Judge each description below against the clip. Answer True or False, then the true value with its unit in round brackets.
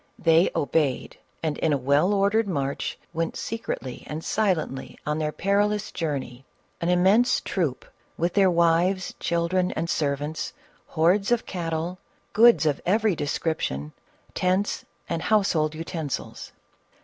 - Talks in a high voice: False (170 Hz)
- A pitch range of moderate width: True (4.1 semitones)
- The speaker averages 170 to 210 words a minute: False (135 wpm)